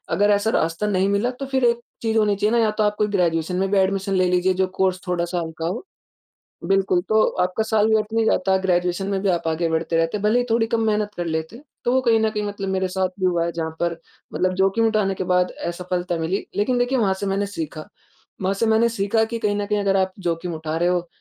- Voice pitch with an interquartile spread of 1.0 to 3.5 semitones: Yes, average, 3.1 semitones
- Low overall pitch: No, high, 195 Hz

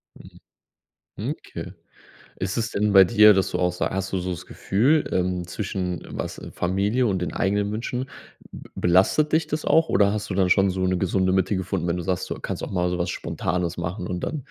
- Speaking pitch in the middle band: No, very low, 95 Hz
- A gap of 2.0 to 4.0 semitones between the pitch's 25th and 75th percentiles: Yes, average, 2.7 semitones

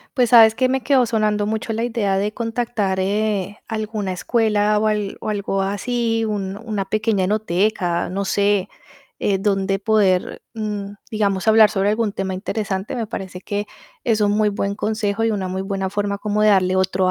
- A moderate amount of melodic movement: No, narrow, 2.1 semitones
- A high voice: Yes, high, 210 Hz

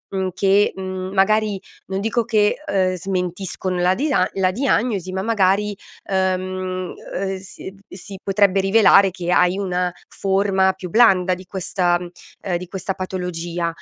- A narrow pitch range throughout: Yes, narrow, 1.3 semitones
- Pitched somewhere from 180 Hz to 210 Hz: Yes, high, 190 Hz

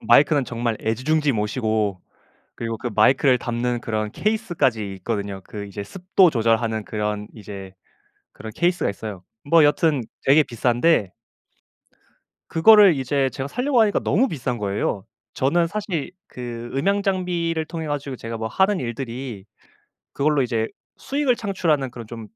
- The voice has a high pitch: No, low, 130 Hz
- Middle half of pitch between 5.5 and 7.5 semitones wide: Yes, wide, 6.8 semitones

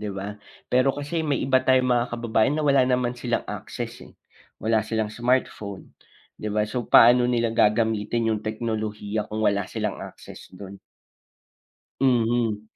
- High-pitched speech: No, low, 115 Hz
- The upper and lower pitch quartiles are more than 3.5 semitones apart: No, average, 2.8 semitones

